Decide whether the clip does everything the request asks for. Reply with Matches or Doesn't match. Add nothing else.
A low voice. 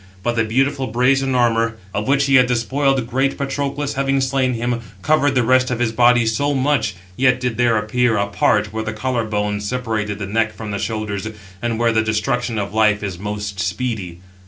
Matches